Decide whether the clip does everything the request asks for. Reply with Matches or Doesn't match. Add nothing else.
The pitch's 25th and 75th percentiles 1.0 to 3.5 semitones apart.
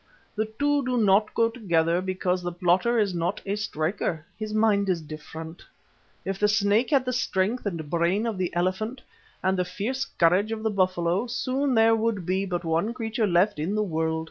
Doesn't match